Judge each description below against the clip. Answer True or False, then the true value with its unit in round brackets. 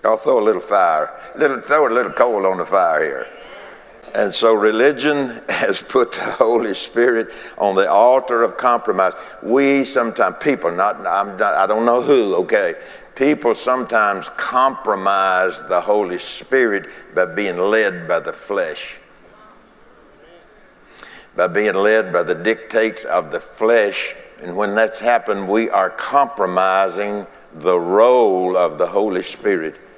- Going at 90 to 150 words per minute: True (145 wpm)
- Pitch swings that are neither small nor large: False (6.2 semitones)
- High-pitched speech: False (120 Hz)